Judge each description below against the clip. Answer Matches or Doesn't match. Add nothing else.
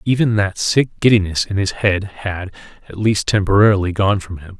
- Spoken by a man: Matches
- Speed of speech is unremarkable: Matches